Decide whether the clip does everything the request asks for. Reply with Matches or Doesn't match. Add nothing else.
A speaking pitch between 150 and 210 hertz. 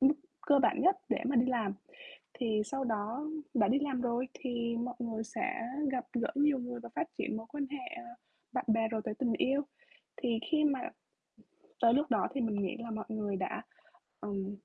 Doesn't match